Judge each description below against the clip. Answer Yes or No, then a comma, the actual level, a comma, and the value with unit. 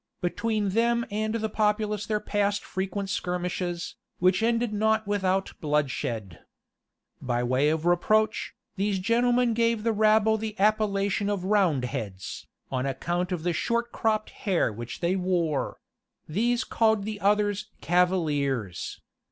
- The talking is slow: Yes, slow, 130 wpm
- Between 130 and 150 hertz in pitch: No, high, 200 Hz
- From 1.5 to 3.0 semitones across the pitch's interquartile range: No, average, 3.9 semitones